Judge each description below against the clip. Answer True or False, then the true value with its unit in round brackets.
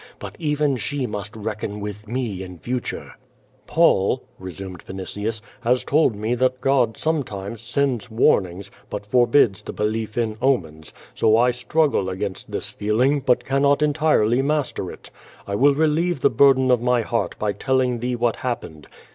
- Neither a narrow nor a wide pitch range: True (4.6 semitones)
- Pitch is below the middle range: True (120 Hz)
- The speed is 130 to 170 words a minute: True (160 wpm)